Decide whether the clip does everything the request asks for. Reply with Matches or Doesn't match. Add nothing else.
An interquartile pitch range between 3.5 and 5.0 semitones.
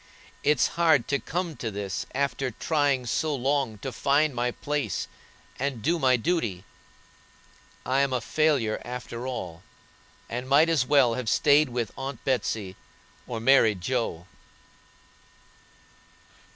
Matches